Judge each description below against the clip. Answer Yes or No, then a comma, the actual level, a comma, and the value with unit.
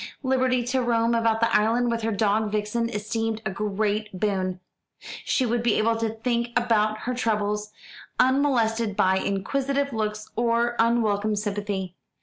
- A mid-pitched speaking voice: No, high, 225 Hz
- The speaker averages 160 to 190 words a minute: No, average, 145 wpm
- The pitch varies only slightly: Yes, narrow, 2.2 semitones